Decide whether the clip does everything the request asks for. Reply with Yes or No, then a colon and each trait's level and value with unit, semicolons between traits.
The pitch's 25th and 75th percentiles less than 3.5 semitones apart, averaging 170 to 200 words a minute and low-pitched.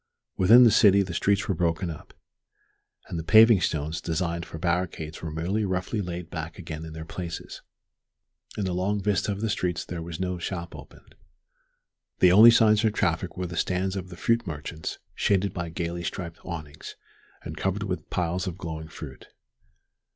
Yes: average, 3.0 semitones; average, 180 wpm; very low, 90 Hz